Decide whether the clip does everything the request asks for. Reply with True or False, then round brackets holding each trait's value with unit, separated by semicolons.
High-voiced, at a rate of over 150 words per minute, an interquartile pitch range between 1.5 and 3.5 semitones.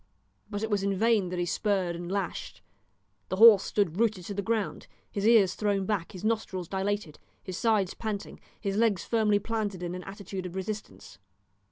True (200 Hz; 185 wpm; 2.7 semitones)